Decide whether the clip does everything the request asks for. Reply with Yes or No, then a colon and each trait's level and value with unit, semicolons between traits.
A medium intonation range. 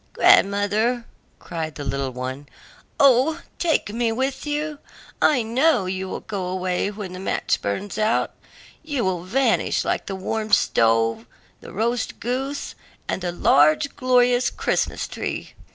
No: wide, 5.8 semitones